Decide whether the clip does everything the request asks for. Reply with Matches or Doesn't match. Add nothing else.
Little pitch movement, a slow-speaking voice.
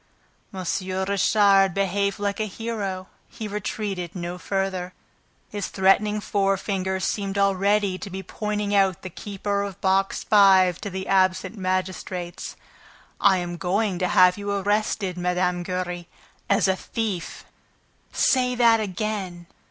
Matches